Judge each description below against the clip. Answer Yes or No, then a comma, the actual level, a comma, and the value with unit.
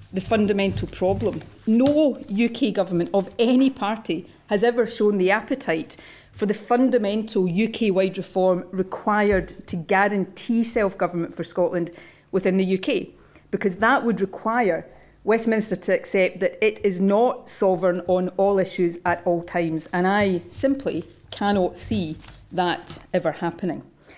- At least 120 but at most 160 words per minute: Yes, average, 140 wpm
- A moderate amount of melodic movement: Yes, average, 3.2 semitones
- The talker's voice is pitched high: Yes, high, 195 Hz